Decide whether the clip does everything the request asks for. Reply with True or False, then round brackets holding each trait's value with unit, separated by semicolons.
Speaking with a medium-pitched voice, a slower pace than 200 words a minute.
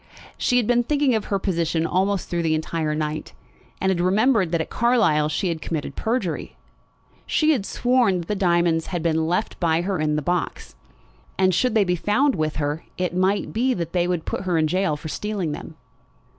False (180 Hz; 205 wpm)